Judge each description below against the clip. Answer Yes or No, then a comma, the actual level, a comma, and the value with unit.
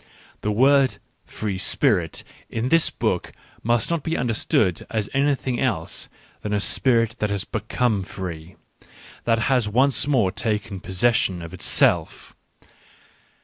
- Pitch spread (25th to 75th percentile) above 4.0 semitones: Yes, average, 4.4 semitones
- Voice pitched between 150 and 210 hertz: No, low, 110 Hz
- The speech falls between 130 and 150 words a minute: Yes, average, 140 wpm